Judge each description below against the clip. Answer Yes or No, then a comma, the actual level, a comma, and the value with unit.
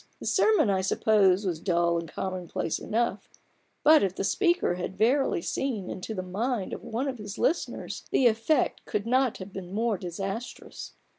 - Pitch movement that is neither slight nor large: Yes, average, 4.8 semitones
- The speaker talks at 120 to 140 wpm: No, average, 170 wpm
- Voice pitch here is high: Yes, high, 205 Hz